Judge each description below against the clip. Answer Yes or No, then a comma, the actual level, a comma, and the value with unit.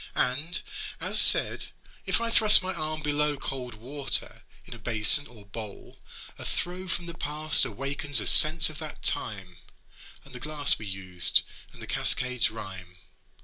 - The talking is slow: No, average, 160 wpm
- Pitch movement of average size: No, wide, 6.2 semitones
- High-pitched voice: No, low, 135 Hz